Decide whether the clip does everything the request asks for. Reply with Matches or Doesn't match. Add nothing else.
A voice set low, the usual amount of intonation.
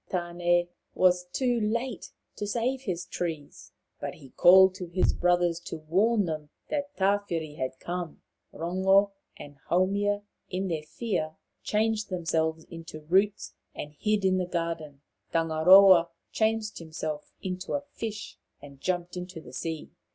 Doesn't match